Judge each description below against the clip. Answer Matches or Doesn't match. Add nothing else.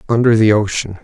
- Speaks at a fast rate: Doesn't match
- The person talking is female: Doesn't match